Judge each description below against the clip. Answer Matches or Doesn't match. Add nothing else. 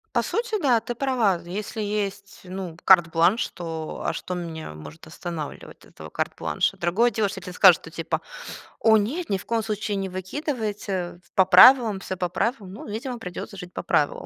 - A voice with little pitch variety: Doesn't match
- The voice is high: Matches